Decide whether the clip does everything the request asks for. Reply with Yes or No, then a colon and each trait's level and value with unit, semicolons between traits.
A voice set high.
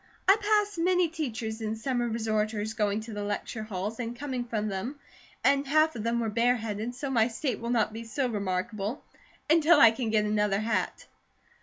Yes: high, 230 Hz